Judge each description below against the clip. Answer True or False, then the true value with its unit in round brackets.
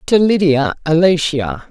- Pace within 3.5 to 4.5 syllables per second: True (4.1 syllables/s)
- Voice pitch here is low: False (160 Hz)